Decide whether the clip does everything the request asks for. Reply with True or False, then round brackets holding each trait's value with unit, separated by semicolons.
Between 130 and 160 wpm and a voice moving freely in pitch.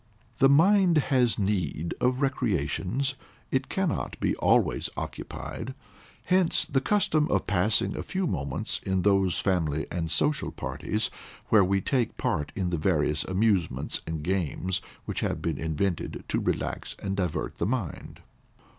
True (145 wpm; 7.9 semitones)